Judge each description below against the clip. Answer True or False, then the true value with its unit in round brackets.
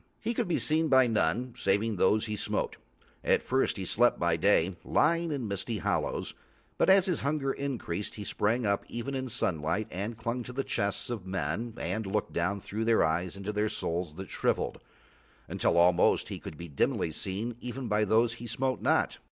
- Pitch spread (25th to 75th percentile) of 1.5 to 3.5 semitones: False (4.5 semitones)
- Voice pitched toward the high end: False (110 Hz)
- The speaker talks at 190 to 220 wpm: True (195 wpm)